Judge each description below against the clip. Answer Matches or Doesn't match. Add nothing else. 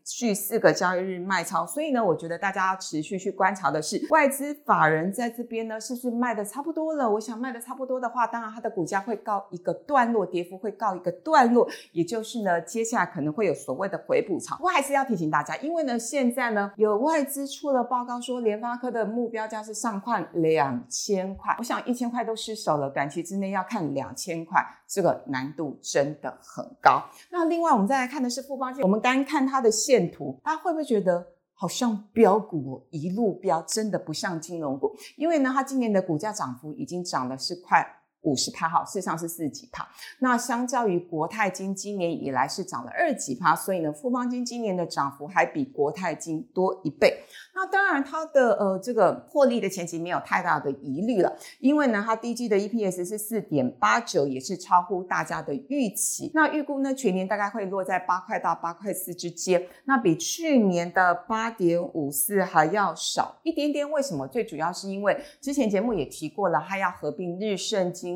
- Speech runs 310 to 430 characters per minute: Matches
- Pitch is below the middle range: Doesn't match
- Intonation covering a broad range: Matches